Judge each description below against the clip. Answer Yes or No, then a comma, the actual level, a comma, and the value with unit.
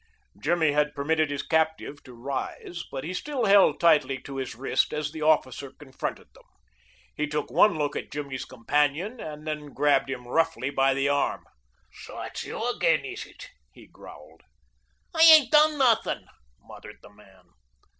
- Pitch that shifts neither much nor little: Yes, average, 3.2 semitones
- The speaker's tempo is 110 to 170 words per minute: Yes, average, 165 wpm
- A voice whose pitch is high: No, medium, 150 Hz